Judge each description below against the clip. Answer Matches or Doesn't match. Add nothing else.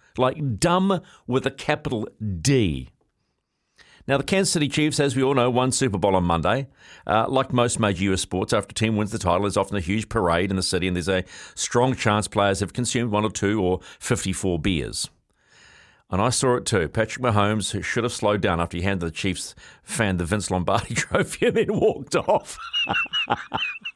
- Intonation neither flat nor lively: Matches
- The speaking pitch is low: Matches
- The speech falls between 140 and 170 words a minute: Doesn't match